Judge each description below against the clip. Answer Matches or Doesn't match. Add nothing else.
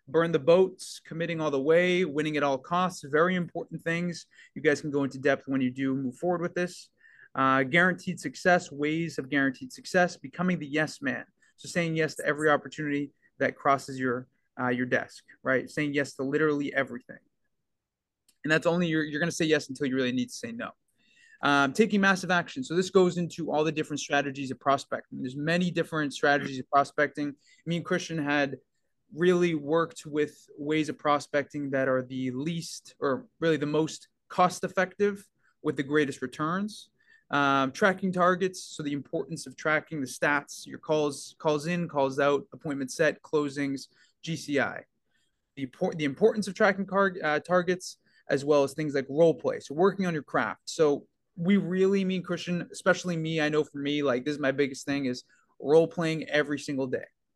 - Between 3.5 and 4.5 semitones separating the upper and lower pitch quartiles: Matches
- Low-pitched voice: Doesn't match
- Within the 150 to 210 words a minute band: Matches